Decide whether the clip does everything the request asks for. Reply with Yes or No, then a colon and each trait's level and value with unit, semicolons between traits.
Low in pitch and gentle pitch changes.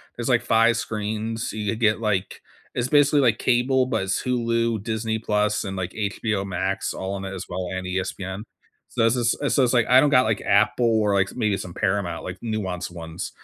No: low, 110 Hz; average, 3.4 semitones